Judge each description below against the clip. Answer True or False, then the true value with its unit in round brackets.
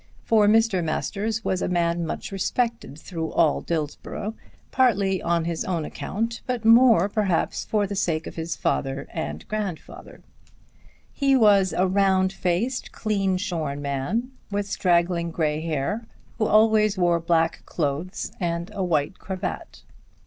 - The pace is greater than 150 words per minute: False (140 wpm)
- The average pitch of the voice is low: False (185 Hz)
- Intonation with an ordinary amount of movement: True (4.2 semitones)